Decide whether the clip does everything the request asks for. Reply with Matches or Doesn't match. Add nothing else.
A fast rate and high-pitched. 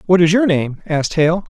Doesn't match